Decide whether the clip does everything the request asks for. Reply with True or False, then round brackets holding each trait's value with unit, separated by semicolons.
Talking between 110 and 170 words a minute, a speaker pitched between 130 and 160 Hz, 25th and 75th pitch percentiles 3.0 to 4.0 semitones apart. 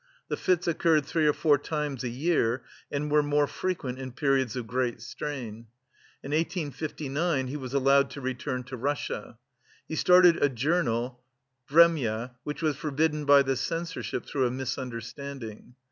True (155 wpm; 140 Hz; 3.3 semitones)